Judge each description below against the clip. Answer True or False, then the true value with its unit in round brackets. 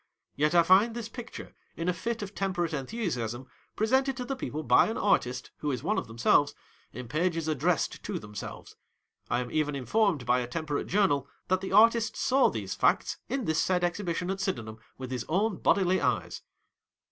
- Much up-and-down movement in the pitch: True (7.5 semitones)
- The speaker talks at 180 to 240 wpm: True (195 wpm)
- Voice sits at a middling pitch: True (170 Hz)